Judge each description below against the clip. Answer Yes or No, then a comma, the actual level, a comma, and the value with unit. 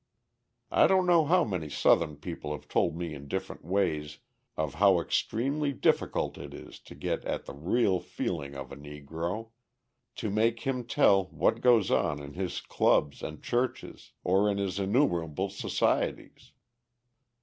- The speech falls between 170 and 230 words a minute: No, average, 155 wpm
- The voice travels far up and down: Yes, wide, 7.1 semitones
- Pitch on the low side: Yes, very low, 95 Hz